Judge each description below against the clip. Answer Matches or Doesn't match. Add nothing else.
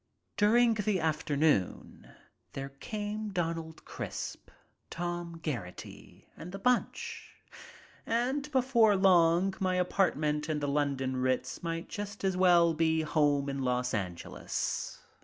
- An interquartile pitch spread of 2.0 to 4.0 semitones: Doesn't match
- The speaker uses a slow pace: Matches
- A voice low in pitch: Doesn't match